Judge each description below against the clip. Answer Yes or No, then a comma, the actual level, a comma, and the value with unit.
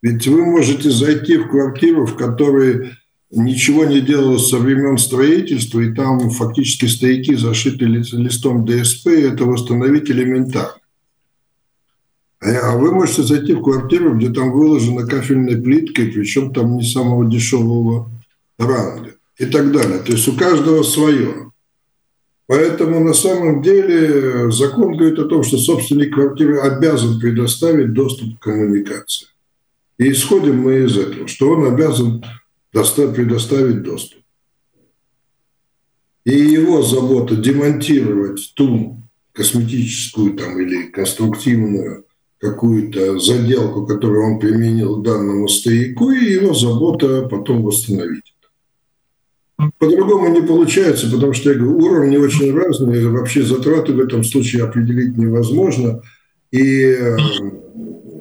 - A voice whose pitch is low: Yes, low, 130 Hz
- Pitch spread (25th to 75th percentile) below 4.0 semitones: Yes, average, 3.5 semitones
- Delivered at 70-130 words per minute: Yes, average, 120 wpm